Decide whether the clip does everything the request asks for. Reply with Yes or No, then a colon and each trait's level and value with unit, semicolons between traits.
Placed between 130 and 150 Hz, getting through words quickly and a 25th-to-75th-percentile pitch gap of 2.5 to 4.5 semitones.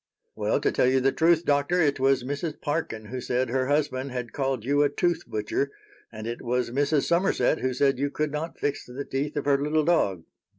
Yes: medium, 140 Hz; fast, 215 wpm; average, 2.8 semitones